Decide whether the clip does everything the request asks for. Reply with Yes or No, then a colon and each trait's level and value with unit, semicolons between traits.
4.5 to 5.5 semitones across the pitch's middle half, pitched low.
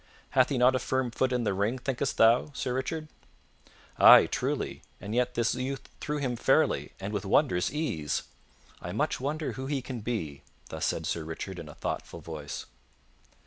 Yes: average, 5.2 semitones; low, 125 Hz